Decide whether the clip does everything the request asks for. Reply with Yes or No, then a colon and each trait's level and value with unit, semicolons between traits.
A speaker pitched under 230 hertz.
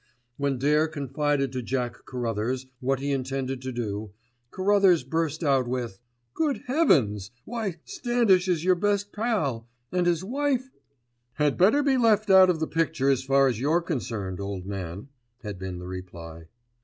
Yes: medium, 140 Hz